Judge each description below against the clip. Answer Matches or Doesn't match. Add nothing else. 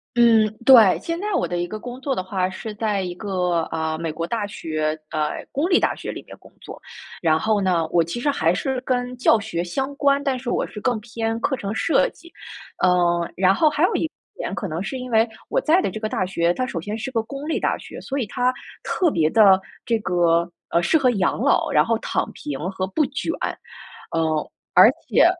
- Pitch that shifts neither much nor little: Doesn't match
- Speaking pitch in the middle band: Doesn't match